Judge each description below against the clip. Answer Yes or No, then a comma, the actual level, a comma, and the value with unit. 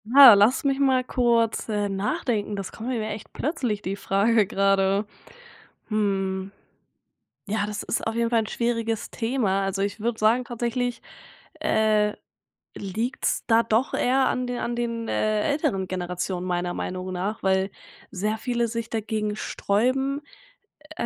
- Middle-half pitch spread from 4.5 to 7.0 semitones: No, average, 3.3 semitones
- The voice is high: Yes, high, 220 Hz